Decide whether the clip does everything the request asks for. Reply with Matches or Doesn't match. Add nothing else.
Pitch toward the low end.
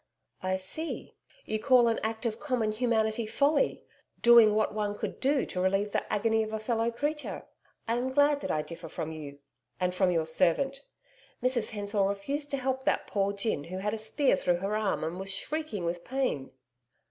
Doesn't match